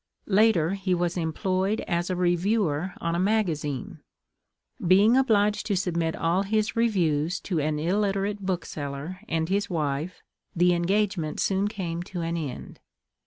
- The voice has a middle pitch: Yes, medium, 180 Hz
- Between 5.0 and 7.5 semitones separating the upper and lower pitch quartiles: No, average, 3.4 semitones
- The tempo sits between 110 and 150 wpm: Yes, average, 140 wpm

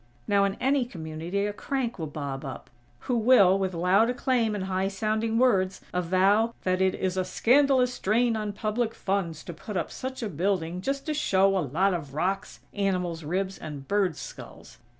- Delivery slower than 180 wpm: No, average, 185 wpm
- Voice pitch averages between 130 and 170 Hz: No, high, 195 Hz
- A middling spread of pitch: Yes, average, 3.9 semitones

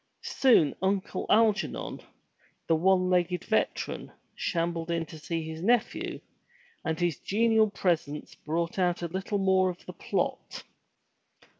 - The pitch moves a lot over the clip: No, average, 2.8 semitones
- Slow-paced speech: Yes, slow, 130 wpm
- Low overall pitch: No, medium, 180 Hz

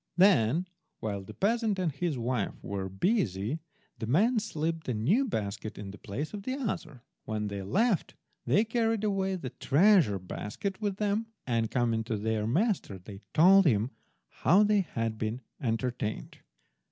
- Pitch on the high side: No, medium, 140 Hz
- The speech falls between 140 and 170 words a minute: Yes, average, 160 wpm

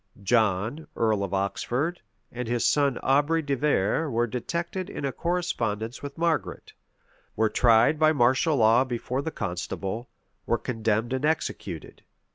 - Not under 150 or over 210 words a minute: No, average, 140 wpm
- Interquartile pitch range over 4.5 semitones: Yes, average, 5.1 semitones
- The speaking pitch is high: No, low, 125 Hz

